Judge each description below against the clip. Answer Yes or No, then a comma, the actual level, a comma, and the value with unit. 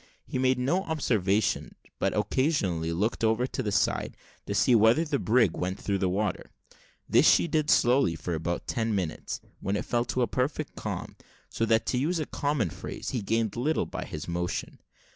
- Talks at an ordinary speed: Yes, average, 180 wpm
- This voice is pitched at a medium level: No, low, 115 Hz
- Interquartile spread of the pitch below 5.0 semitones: No, average, 5.3 semitones